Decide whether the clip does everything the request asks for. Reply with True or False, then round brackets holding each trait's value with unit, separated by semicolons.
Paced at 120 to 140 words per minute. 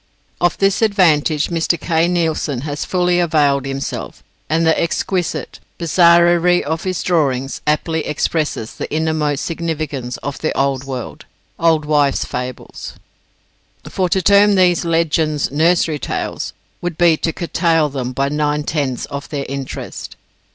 True (135 wpm)